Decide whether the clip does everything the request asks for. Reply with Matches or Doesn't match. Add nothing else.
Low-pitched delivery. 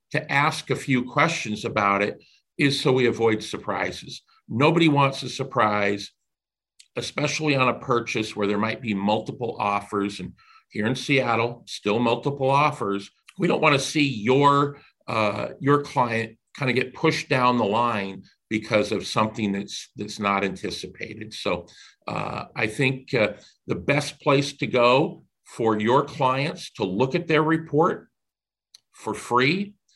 Matches